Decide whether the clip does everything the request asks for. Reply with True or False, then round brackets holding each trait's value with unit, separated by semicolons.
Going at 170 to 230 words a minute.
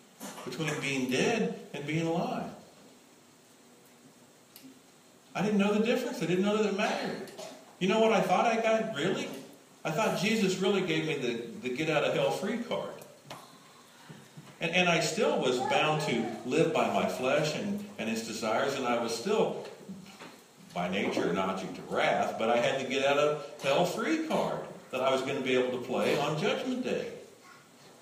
True (180 wpm)